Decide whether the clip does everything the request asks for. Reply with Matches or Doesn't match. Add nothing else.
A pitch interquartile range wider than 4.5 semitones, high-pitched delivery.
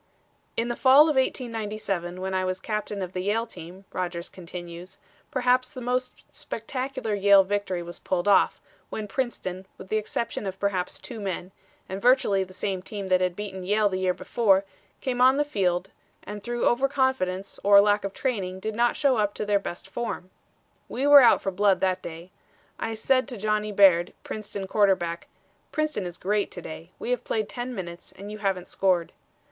Doesn't match